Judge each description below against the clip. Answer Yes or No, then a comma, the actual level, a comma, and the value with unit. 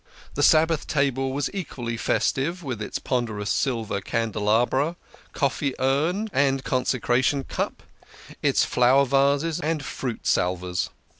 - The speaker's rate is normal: No, slow, 120 wpm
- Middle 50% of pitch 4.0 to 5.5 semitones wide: No, average, 3.5 semitones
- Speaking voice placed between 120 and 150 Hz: Yes, low, 135 Hz